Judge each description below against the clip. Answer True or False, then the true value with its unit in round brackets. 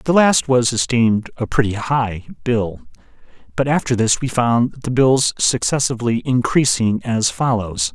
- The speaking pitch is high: False (120 Hz)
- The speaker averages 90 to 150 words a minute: True (145 wpm)